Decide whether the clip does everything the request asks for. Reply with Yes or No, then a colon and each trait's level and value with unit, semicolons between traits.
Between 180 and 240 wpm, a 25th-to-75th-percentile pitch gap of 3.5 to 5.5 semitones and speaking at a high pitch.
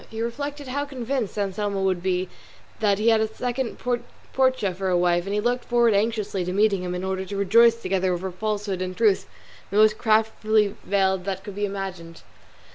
No: average, 195 wpm; average, 3.1 semitones; high, 205 Hz